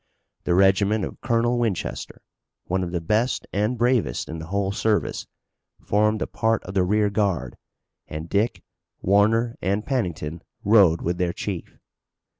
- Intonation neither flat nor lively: Yes, average, 3.9 semitones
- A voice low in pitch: Yes, low, 100 Hz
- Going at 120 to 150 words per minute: Yes, average, 145 wpm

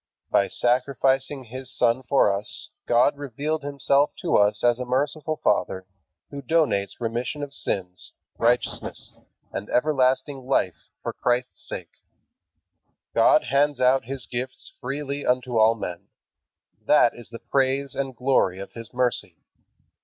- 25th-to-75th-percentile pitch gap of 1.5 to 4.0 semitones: Yes, average, 3.0 semitones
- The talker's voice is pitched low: Yes, low, 130 Hz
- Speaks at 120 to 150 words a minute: Yes, slow, 135 wpm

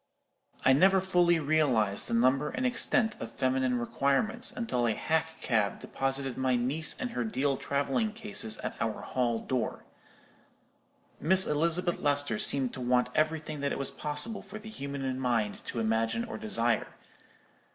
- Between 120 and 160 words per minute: Yes, average, 155 wpm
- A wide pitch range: Yes, wide, 6.0 semitones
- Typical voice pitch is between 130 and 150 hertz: Yes, medium, 140 Hz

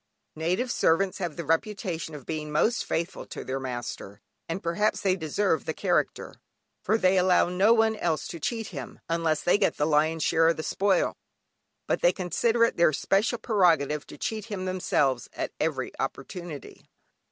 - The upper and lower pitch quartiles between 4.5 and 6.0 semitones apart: No, average, 4.1 semitones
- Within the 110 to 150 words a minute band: No, average, 175 wpm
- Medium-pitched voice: Yes, medium, 175 Hz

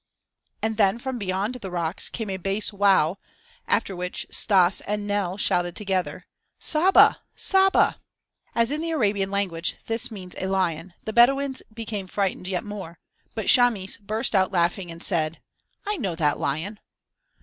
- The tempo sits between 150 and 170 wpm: Yes, average, 155 wpm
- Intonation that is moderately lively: Yes, average, 3.6 semitones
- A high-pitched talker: Yes, high, 195 Hz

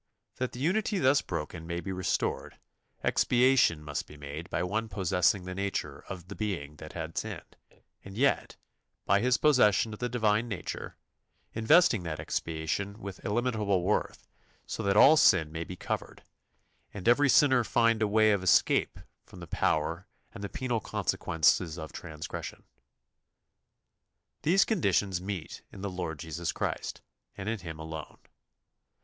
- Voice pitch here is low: Yes, low, 100 Hz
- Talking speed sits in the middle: Yes, average, 155 wpm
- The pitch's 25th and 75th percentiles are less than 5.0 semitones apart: No, average, 5.3 semitones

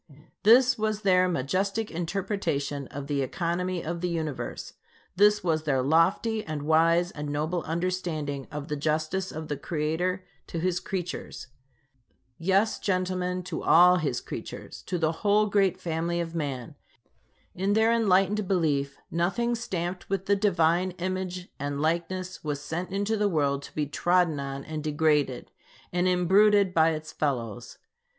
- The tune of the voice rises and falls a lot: No, average, 3.6 semitones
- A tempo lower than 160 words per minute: Yes, average, 150 wpm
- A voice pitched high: No, medium, 175 Hz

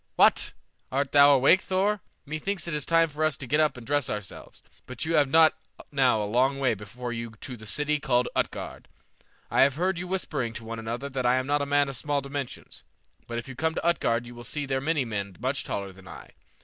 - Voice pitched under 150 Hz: Yes, low, 135 Hz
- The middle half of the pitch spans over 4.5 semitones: No, average, 4.0 semitones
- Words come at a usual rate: No, fast, 240 wpm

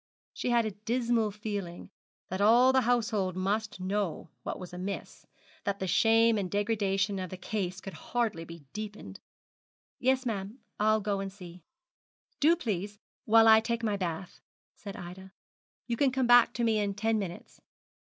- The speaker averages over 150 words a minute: Yes, average, 165 wpm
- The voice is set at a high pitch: Yes, high, 210 Hz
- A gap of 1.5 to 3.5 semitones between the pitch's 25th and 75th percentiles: Yes, average, 3.1 semitones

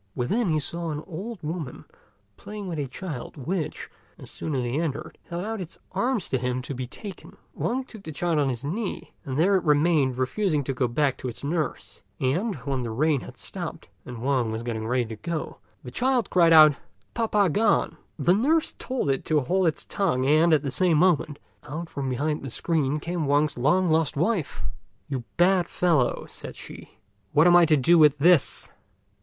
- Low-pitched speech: No, medium, 155 Hz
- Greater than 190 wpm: Yes, average, 200 wpm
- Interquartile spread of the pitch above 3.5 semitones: Yes, average, 4.9 semitones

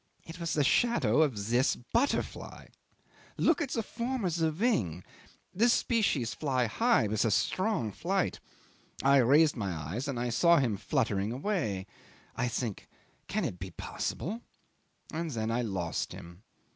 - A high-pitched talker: No, low, 135 Hz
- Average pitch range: No, wide, 8.9 semitones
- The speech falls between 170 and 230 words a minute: No, average, 155 wpm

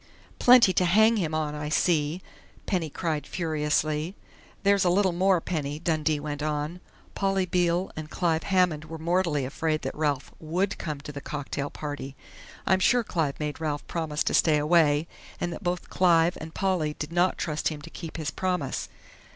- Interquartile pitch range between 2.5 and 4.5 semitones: Yes, average, 3.1 semitones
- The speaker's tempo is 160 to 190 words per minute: Yes, average, 175 wpm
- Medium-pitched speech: Yes, medium, 160 Hz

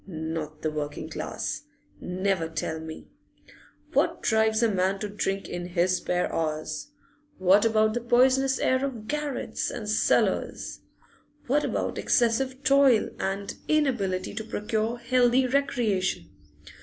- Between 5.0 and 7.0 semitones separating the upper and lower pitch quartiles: Yes, wide, 5.5 semitones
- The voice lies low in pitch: No, high, 215 Hz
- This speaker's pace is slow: Yes, slow, 130 wpm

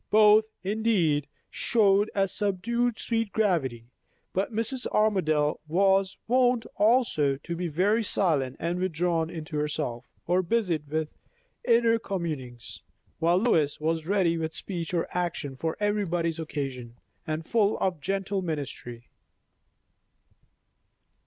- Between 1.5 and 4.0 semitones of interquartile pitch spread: No, average, 5.1 semitones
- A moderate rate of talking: No, slow, 120 wpm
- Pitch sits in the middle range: Yes, medium, 175 Hz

